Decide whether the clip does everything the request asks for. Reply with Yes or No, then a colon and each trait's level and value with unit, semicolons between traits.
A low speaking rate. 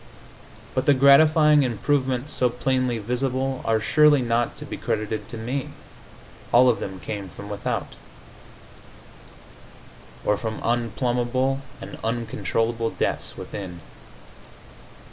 Yes: slow, 110 wpm